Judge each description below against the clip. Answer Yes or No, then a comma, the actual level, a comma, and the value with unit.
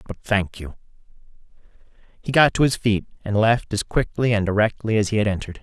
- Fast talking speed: No, average, 190 wpm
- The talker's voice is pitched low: Yes, low, 105 Hz